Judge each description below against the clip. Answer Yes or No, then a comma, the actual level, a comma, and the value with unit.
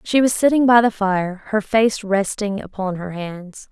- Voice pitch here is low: No, high, 205 Hz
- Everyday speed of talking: Yes, average, 195 wpm